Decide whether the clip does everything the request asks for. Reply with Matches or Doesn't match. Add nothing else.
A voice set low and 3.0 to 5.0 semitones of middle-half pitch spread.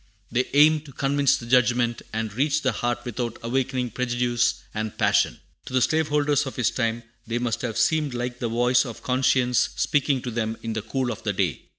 Doesn't match